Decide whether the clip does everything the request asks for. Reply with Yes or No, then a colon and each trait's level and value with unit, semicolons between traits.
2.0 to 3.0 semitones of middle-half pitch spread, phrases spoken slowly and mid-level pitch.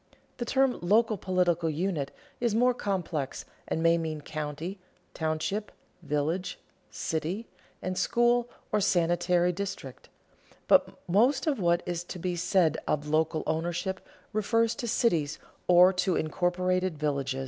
No: average, 4.0 semitones; slow, 130 wpm; medium, 180 Hz